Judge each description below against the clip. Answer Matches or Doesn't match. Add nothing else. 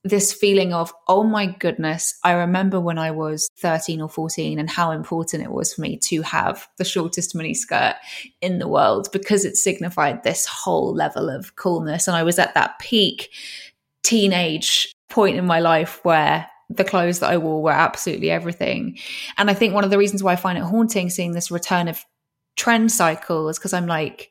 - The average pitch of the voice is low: Doesn't match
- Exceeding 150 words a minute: Matches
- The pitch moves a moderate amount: Matches